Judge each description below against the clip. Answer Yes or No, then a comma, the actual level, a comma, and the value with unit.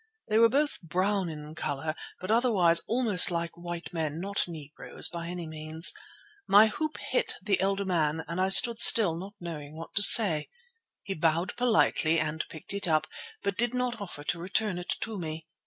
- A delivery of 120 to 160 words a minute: No, average, 185 wpm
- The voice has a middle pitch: Yes, medium, 180 Hz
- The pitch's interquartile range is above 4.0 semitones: Yes, average, 4.4 semitones